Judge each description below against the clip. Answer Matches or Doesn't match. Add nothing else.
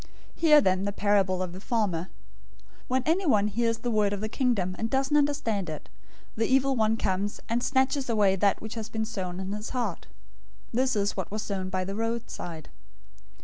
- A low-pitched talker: Doesn't match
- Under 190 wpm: Doesn't match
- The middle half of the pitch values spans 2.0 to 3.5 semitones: Doesn't match